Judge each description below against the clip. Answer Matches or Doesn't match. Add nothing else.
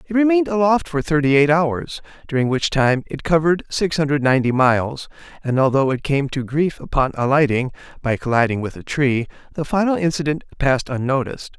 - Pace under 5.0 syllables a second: Doesn't match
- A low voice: Doesn't match